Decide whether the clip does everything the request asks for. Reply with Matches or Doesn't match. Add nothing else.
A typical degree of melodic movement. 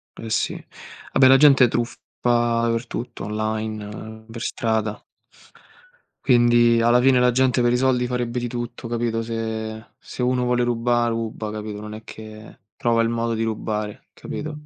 Doesn't match